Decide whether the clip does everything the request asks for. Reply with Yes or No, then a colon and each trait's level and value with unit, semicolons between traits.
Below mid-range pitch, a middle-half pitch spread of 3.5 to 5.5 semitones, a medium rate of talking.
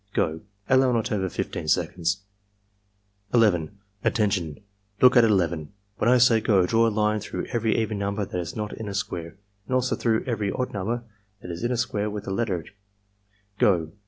Yes: low, 105 Hz; average, 3.9 semitones; average, 190 wpm